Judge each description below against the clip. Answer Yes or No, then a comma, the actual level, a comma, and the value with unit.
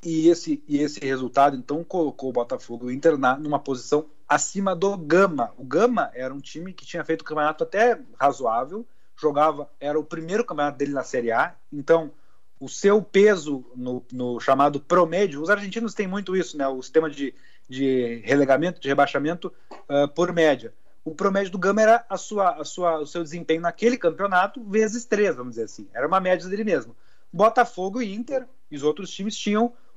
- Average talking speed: No, fast, 190 wpm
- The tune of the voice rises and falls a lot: Yes, wide, 6.0 semitones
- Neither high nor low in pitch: Yes, medium, 165 Hz